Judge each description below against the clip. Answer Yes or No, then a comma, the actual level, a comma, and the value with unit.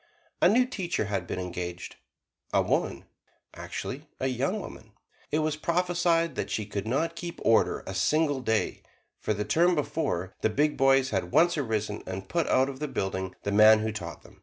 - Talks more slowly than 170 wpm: No, average, 185 wpm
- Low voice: Yes, low, 130 Hz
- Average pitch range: No, wide, 7.9 semitones